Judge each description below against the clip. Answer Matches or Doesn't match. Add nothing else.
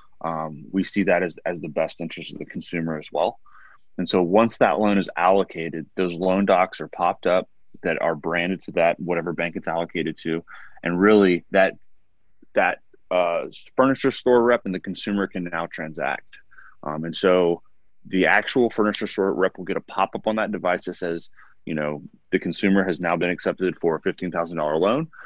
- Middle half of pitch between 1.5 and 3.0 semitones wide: Matches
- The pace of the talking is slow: Doesn't match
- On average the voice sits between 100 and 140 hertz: Doesn't match